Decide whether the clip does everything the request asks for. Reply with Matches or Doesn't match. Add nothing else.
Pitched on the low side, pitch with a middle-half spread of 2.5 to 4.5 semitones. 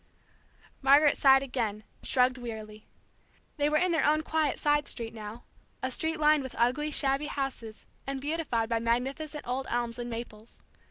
Doesn't match